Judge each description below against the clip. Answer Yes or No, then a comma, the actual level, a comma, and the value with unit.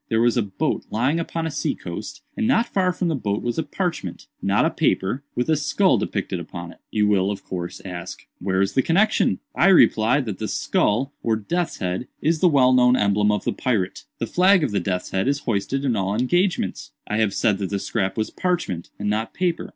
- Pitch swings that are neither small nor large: No, wide, 8.2 semitones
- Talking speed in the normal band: No, fast, 220 wpm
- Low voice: Yes, low, 115 Hz